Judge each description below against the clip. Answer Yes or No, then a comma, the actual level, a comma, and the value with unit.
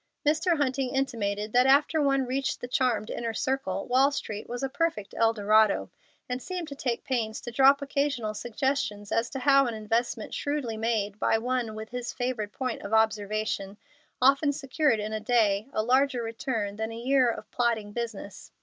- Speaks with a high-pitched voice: Yes, high, 240 Hz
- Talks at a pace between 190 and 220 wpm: No, average, 175 wpm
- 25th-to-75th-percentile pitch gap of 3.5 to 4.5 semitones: Yes, average, 3.8 semitones